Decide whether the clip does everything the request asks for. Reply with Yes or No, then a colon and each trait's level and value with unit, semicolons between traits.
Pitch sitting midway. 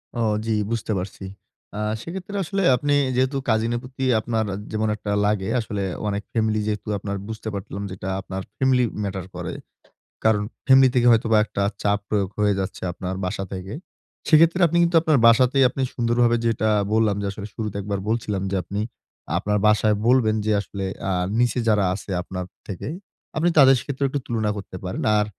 No: low, 110 Hz